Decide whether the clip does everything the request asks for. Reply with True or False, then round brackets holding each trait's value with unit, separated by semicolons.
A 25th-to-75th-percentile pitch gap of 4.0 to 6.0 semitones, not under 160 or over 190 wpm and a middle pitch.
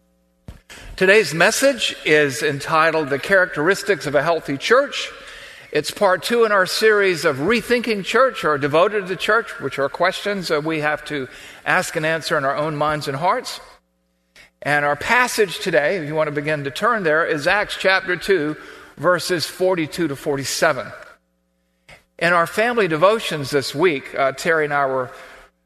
True (5.4 semitones; 165 wpm; 155 Hz)